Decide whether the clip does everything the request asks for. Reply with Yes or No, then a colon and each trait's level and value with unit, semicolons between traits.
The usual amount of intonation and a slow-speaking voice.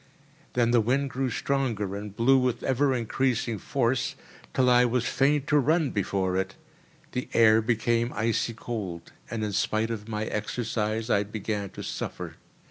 No: average, 3.1 semitones; average, 160 wpm